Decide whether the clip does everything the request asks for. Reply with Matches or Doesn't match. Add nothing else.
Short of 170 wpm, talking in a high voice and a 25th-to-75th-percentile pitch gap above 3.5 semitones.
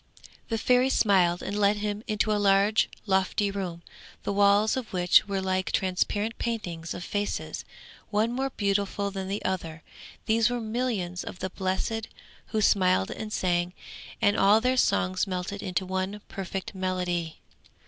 Doesn't match